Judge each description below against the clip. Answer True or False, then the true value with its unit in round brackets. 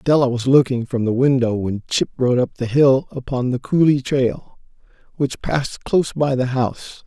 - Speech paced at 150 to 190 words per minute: True (185 wpm)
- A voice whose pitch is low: True (130 Hz)